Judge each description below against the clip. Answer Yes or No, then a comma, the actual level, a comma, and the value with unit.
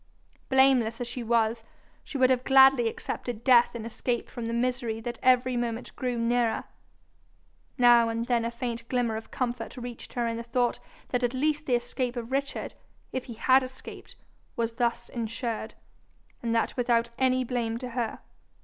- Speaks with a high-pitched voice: Yes, high, 240 Hz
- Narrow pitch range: Yes, narrow, 1.5 semitones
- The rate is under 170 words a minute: No, average, 175 wpm